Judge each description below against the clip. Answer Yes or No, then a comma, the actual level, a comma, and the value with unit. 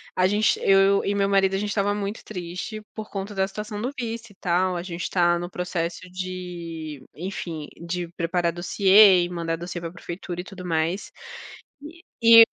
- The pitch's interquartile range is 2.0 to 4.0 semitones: Yes, narrow, 2.6 semitones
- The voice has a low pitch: No, medium, 185 Hz